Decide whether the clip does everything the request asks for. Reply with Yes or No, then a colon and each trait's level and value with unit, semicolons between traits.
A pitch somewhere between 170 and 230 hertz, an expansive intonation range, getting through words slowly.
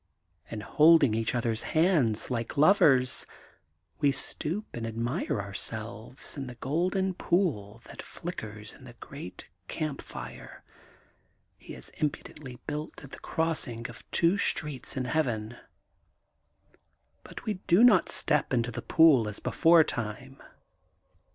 No: low, 135 Hz; wide, 5.8 semitones; slow, 130 wpm